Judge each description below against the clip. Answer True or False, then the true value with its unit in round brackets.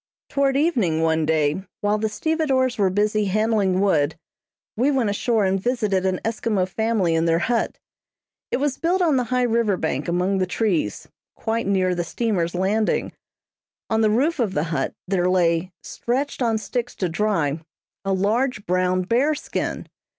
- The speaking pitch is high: True (205 Hz)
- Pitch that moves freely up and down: False (4.7 semitones)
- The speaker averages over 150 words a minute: True (165 wpm)